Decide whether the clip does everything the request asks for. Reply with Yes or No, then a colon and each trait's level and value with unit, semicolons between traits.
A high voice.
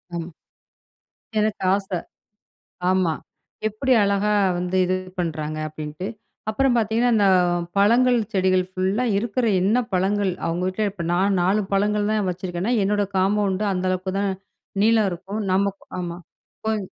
Yes: high, 195 Hz